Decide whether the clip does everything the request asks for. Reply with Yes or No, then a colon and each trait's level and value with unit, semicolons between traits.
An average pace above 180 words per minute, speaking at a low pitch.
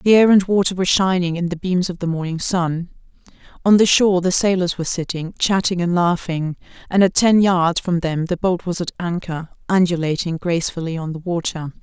No: average, 200 wpm; medium, 175 Hz